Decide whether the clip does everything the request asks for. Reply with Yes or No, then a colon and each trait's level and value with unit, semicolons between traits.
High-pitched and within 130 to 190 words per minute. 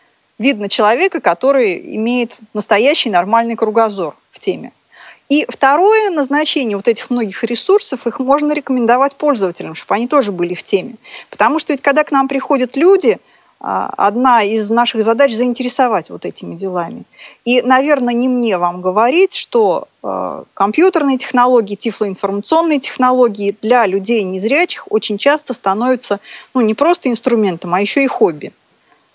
Yes: high, 245 Hz; average, 140 wpm